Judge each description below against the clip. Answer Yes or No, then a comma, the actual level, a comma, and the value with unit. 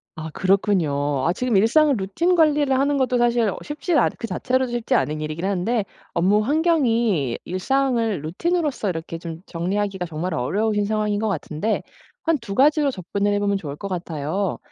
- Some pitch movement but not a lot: No, wide, 6.7 semitones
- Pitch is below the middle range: No, high, 205 Hz